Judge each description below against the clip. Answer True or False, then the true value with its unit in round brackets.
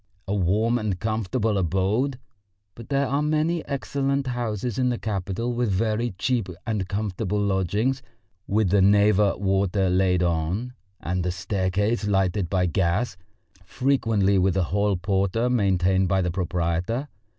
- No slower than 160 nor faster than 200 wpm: False (140 wpm)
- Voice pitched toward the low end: True (100 Hz)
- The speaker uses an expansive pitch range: False (4.0 semitones)